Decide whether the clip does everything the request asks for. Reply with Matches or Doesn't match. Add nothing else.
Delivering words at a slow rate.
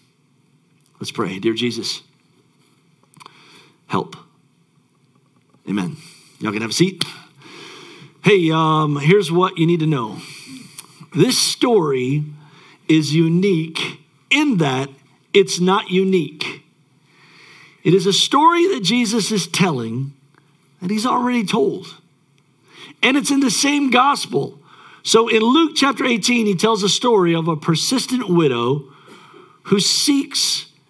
Matches